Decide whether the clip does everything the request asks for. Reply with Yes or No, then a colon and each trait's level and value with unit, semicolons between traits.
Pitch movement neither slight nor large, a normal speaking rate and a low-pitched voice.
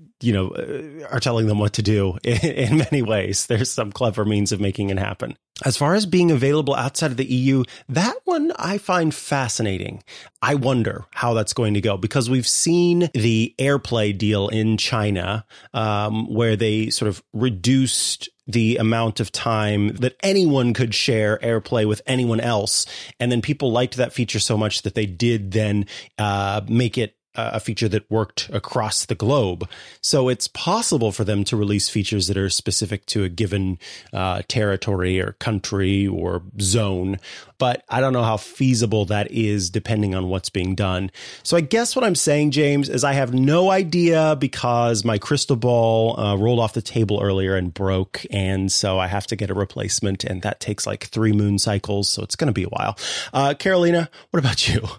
Yes: average, 4.1 semitones; average, 190 wpm; low, 110 Hz